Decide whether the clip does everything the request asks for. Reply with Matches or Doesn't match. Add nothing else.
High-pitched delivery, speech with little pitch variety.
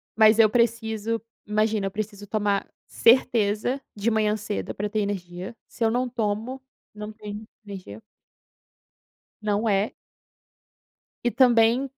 Matches